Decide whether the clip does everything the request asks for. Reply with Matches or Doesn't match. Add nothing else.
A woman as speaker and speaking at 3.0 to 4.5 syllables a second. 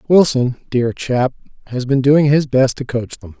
Doesn't match